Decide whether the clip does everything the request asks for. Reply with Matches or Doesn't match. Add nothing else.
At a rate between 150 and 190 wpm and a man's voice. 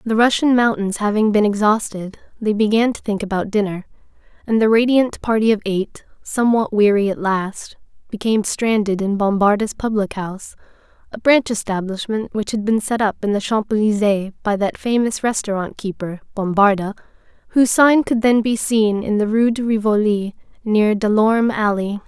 Doesn't match